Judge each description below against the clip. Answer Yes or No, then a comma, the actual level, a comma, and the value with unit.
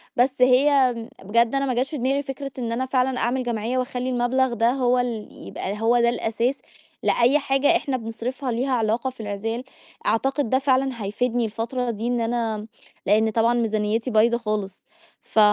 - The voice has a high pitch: Yes, high, 240 Hz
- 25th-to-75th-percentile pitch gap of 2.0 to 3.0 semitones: Yes, narrow, 2.5 semitones